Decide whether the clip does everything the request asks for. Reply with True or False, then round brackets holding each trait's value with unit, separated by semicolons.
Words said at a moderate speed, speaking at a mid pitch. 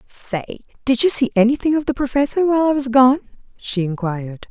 False (185 wpm; 250 Hz)